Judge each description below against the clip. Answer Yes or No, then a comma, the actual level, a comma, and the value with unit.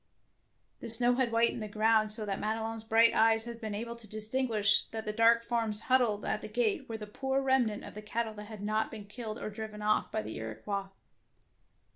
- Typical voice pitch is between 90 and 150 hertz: No, high, 220 Hz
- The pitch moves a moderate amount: No, narrow, 1.7 semitones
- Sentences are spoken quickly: Yes, fast, 225 wpm